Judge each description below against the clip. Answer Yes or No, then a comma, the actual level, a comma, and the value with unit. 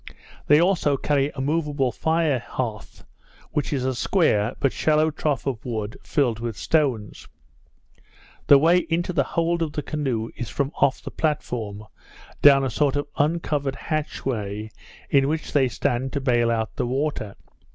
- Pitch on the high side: No, medium, 140 Hz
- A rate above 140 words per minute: Yes, average, 160 wpm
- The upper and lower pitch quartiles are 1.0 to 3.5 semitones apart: No, average, 4.2 semitones